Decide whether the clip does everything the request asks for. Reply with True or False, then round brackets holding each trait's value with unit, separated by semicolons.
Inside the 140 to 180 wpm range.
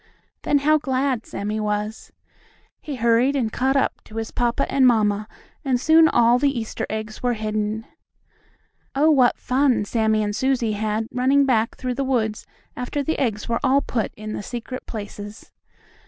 True (170 wpm)